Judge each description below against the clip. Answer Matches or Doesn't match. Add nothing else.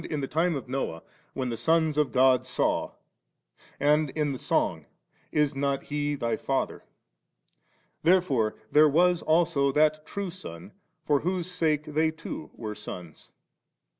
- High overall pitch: Doesn't match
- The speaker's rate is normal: Matches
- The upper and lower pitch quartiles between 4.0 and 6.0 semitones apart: Doesn't match